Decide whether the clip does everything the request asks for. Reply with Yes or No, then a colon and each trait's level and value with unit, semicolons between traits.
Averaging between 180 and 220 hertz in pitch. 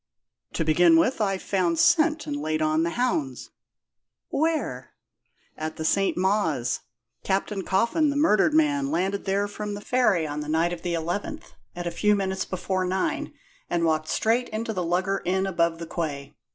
Yes: high, 190 Hz